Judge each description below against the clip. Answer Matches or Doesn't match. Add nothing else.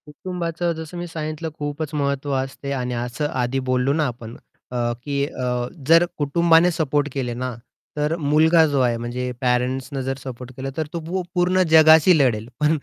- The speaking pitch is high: Doesn't match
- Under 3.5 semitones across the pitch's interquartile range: Doesn't match